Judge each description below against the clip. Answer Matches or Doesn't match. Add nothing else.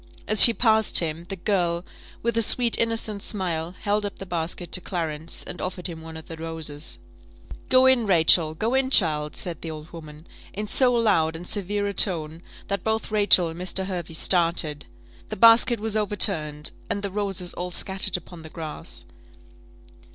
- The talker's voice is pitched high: Doesn't match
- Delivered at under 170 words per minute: Doesn't match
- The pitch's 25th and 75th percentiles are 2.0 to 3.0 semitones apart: Doesn't match